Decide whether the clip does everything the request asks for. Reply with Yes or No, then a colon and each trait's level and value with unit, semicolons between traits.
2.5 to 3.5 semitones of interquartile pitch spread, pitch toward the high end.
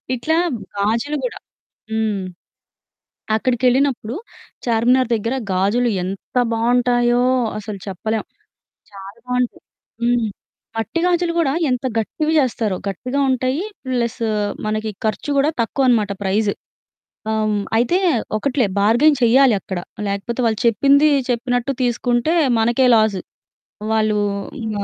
Yes: average, 3.0 semitones; high, 235 Hz